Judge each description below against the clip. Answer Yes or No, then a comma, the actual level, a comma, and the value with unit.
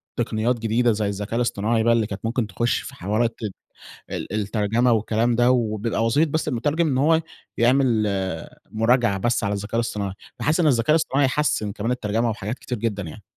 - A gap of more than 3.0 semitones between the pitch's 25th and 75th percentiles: No, average, 2.7 semitones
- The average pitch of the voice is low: Yes, low, 115 Hz